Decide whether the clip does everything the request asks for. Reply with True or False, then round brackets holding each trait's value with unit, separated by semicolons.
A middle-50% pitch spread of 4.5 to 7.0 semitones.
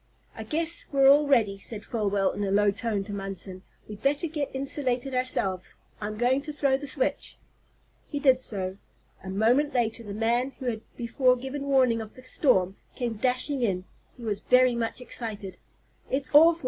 True (4.8 semitones)